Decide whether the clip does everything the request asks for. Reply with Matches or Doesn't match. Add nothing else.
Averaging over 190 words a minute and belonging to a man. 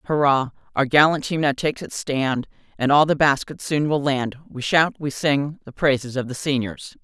Doesn't match